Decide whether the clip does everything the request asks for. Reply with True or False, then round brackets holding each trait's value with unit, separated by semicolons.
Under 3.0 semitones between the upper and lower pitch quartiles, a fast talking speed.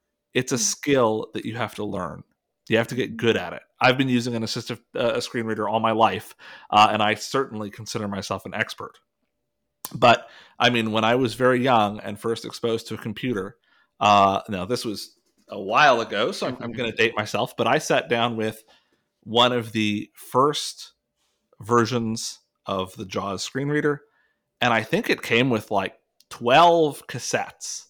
False (2.5 semitones; 185 wpm)